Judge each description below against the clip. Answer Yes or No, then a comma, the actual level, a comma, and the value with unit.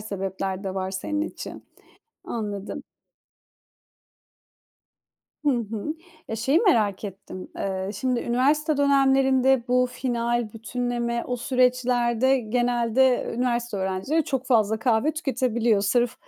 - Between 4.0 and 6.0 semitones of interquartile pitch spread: No, average, 3.5 semitones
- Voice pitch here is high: Yes, high, 240 Hz